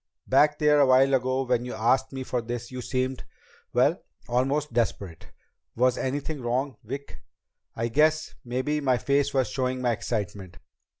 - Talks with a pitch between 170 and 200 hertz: No, low, 130 Hz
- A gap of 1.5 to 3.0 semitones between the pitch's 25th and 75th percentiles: Yes, narrow, 2.4 semitones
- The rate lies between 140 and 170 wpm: Yes, average, 160 wpm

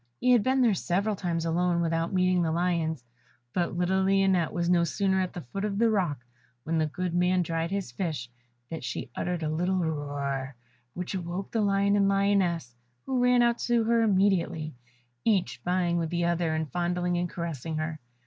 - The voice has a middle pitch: Yes, medium, 175 Hz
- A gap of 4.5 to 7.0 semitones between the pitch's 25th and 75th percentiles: No, average, 3.1 semitones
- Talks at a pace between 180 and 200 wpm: Yes, average, 190 wpm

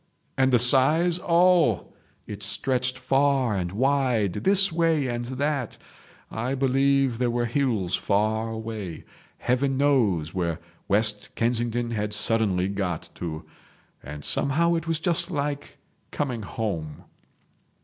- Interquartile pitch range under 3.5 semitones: No, average, 5.1 semitones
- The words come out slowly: Yes, slow, 125 wpm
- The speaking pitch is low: Yes, low, 120 Hz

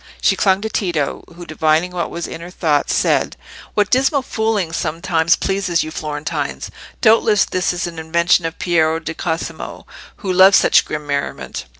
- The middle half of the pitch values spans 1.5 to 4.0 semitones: Yes, average, 3.3 semitones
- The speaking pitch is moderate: Yes, medium, 170 Hz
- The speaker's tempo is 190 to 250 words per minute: No, average, 170 wpm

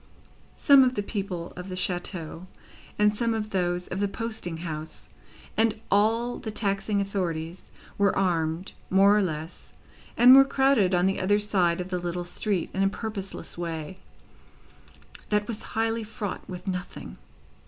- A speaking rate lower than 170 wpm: Yes, average, 155 wpm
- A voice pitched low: No, high, 195 Hz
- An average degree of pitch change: Yes, average, 3.2 semitones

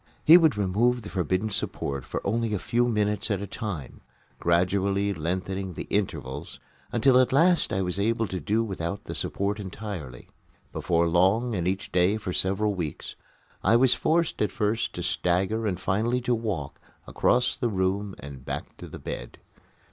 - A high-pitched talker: No, low, 100 Hz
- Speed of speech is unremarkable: Yes, average, 170 wpm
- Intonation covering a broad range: No, average, 3.8 semitones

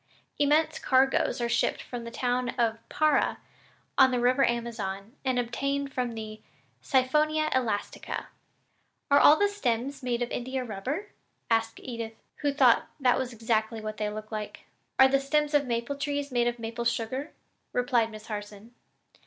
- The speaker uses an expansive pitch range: No, average, 3.4 semitones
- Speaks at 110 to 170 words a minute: Yes, average, 160 wpm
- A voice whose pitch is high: Yes, high, 245 Hz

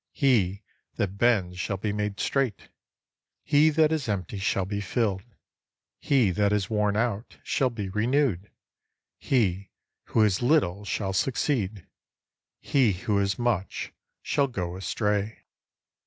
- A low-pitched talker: Yes, low, 105 Hz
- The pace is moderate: No, slow, 130 wpm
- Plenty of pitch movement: No, average, 3.9 semitones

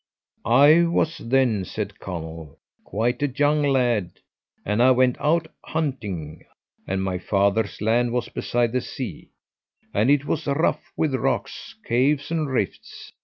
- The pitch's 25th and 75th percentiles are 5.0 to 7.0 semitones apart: Yes, wide, 5.6 semitones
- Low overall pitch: Yes, low, 120 Hz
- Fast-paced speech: No, average, 140 wpm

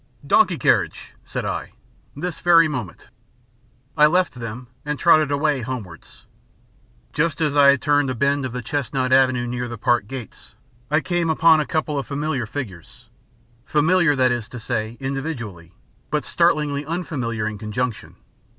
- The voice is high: No, low, 135 Hz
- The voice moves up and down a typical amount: Yes, average, 3.9 semitones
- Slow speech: No, average, 160 wpm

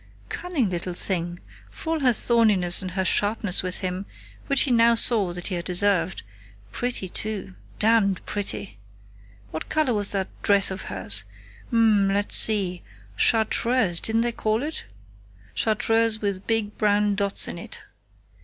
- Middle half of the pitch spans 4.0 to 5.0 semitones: No, average, 3.6 semitones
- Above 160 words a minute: No, average, 150 wpm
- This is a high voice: Yes, high, 205 Hz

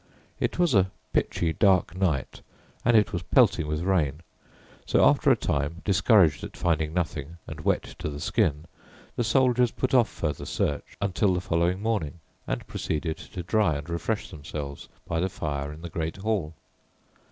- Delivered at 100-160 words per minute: No, average, 170 wpm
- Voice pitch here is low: Yes, very low, 85 Hz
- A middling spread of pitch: Yes, average, 4.5 semitones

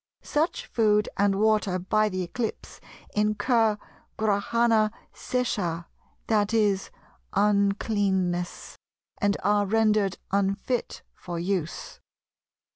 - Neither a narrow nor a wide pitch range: No, narrow, 2.1 semitones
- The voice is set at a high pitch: Yes, high, 205 Hz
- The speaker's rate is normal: No, slow, 90 wpm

